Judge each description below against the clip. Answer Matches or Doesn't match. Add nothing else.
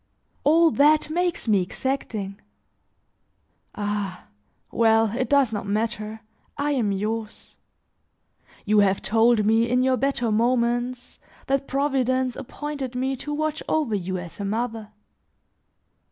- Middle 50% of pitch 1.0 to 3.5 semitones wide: Doesn't match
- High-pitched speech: Matches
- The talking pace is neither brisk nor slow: Doesn't match